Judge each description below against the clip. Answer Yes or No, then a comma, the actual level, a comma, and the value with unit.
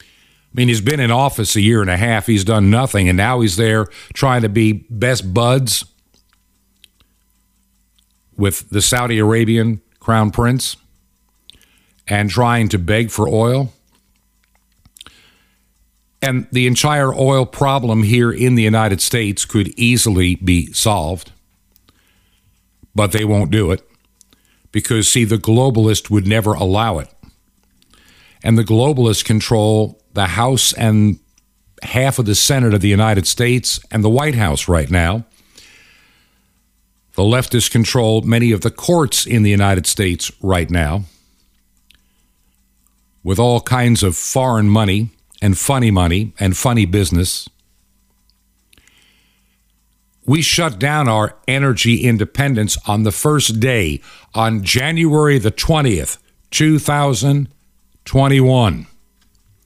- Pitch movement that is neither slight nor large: Yes, average, 3.8 semitones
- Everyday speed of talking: No, slow, 125 wpm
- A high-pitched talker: No, low, 110 Hz